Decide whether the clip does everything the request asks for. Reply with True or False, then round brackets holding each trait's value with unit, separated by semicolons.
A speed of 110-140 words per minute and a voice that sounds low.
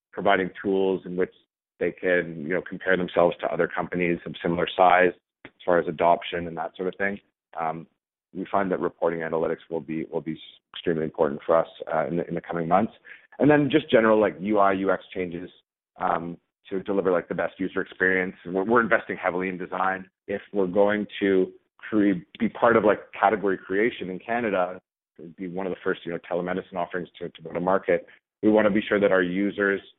False (205 wpm; 95 Hz)